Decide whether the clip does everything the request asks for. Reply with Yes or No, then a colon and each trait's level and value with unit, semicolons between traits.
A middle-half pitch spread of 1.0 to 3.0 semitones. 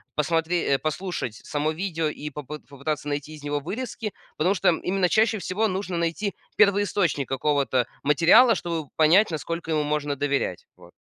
No: average, 4.1 semitones